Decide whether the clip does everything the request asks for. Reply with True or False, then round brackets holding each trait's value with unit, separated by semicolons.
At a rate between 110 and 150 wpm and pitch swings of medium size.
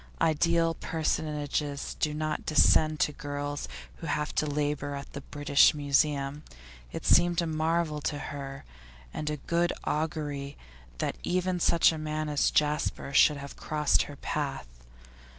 False (145 wpm; 1.6 semitones)